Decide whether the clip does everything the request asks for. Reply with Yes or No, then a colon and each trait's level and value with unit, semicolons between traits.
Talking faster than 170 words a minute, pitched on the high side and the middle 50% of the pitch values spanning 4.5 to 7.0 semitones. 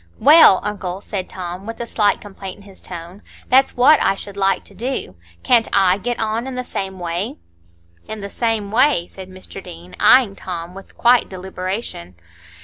No: average, 180 wpm; high, 200 Hz; average, 3.7 semitones